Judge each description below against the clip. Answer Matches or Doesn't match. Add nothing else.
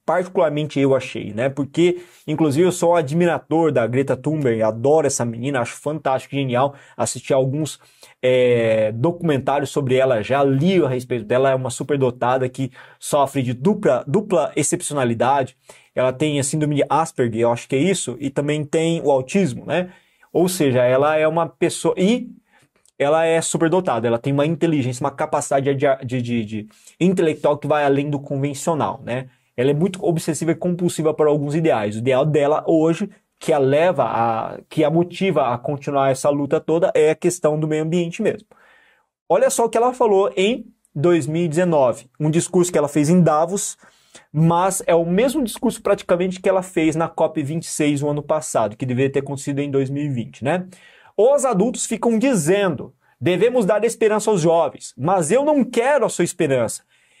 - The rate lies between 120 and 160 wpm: Doesn't match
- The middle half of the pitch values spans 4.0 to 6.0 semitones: Matches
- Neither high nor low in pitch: Matches